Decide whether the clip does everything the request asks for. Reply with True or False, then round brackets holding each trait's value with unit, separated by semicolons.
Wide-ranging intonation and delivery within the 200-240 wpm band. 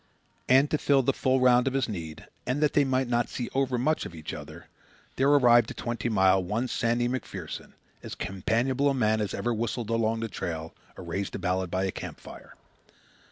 False (5.0 semitones; 205 wpm)